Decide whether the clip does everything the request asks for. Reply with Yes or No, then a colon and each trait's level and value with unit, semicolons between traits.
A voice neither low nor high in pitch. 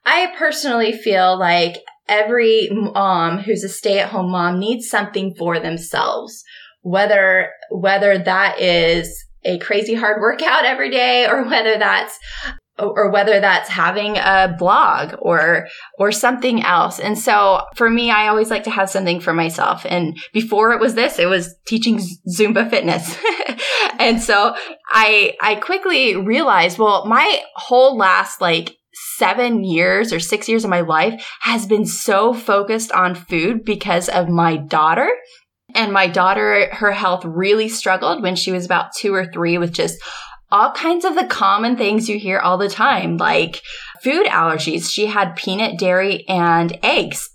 No: high, 205 Hz